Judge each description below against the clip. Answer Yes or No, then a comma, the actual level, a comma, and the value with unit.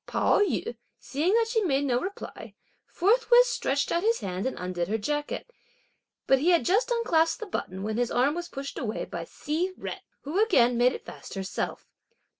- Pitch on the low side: No, very high, 295 Hz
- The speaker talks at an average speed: Yes, average, 190 wpm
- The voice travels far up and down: Yes, wide, 8.6 semitones